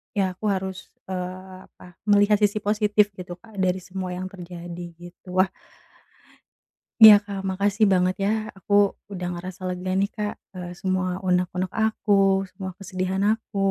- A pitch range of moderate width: No, narrow, 1.9 semitones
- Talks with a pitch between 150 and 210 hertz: Yes, medium, 185 Hz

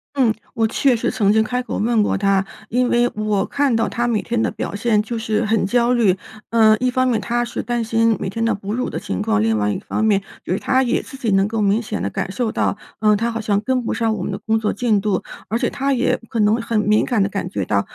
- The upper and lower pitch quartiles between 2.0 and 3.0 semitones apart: Yes, average, 2.7 semitones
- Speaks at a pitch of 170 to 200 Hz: No, high, 220 Hz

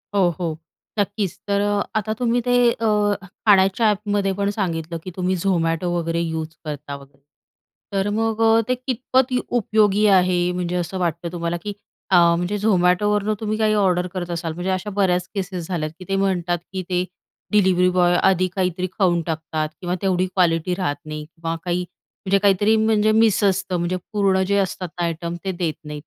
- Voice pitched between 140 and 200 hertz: Yes, medium, 185 Hz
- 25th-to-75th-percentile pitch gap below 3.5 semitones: Yes, average, 3.0 semitones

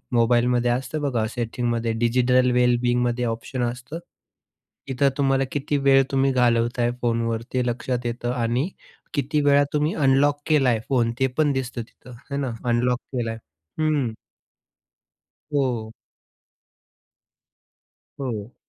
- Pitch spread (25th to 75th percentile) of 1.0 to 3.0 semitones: Yes, narrow, 2.4 semitones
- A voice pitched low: Yes, low, 125 Hz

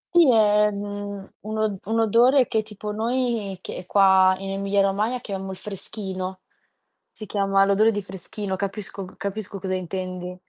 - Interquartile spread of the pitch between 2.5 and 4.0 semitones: No, narrow, 2.0 semitones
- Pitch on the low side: No, high, 200 Hz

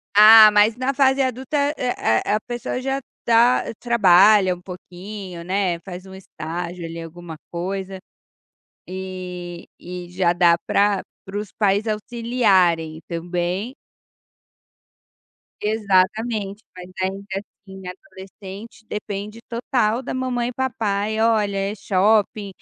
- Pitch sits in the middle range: No, high, 200 Hz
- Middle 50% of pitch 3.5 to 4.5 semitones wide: Yes, average, 3.8 semitones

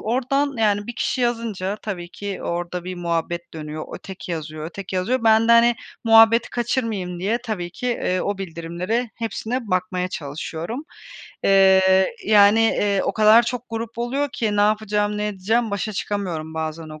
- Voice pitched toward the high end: Yes, high, 205 Hz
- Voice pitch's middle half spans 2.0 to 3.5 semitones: No, average, 4.3 semitones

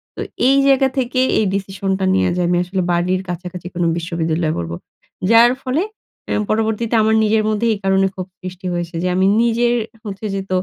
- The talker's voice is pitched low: No, high, 190 Hz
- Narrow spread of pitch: No, average, 3.7 semitones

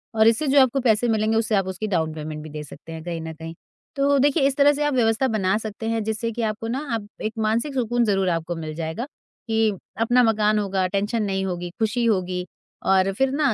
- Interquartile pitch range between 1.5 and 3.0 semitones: No, average, 4.3 semitones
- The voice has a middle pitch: No, high, 215 Hz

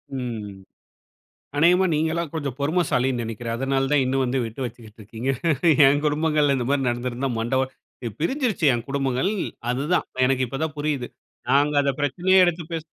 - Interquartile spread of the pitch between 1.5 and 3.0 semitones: No, average, 3.8 semitones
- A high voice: No, low, 135 Hz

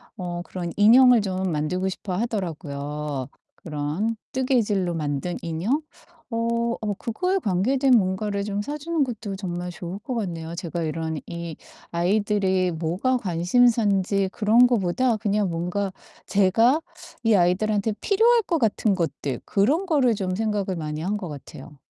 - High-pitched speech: Yes, high, 195 Hz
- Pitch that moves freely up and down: No, average, 4.9 semitones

